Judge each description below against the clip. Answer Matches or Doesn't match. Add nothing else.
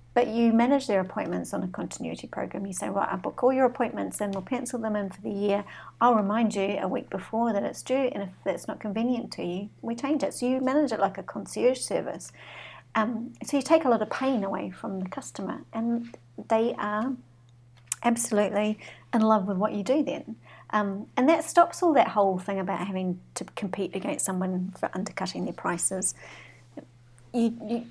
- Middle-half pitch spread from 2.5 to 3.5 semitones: Doesn't match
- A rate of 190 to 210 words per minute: Matches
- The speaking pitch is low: Doesn't match